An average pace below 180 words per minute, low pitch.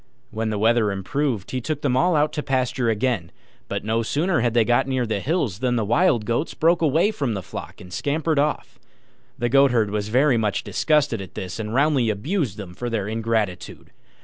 No: average, 200 wpm; low, 120 Hz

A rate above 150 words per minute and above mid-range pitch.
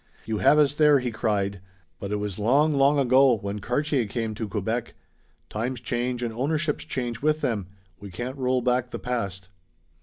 No: average, 180 wpm; low, 120 Hz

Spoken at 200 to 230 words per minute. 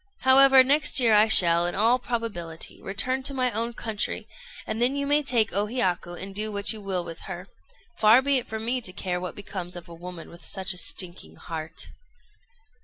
Yes: fast, 205 wpm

